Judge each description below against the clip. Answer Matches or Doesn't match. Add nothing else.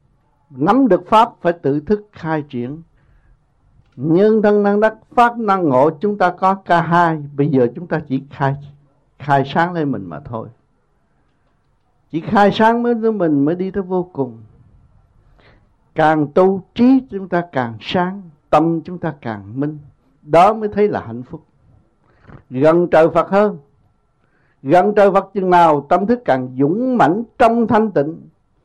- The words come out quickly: Doesn't match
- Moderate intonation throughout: Doesn't match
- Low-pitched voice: Doesn't match